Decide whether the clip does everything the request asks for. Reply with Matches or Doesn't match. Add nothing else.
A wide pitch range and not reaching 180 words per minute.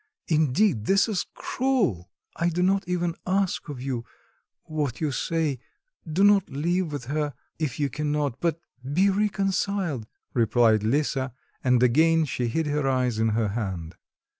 Matches